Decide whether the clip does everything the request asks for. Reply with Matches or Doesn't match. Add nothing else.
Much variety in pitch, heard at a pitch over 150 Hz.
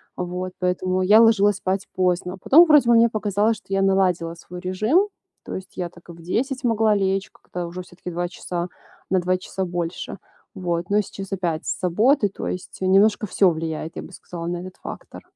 Doesn't match